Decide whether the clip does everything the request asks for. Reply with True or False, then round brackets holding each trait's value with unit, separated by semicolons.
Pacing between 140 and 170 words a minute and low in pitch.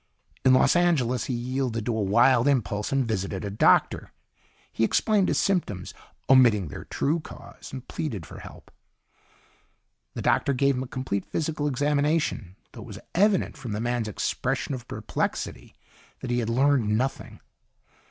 True (160 wpm; 130 Hz)